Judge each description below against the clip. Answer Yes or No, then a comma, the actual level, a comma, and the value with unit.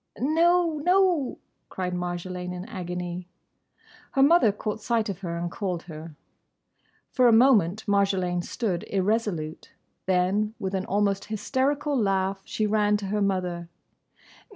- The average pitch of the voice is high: Yes, high, 200 Hz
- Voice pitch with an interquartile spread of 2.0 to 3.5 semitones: No, average, 4.2 semitones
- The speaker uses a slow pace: Yes, slow, 130 wpm